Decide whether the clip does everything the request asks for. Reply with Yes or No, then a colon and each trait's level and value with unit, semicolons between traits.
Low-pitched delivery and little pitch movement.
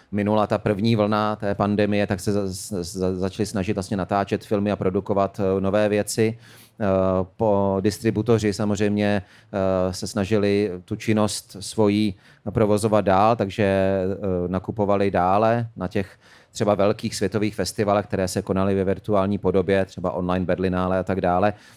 Yes: low, 100 Hz; narrow, 1.8 semitones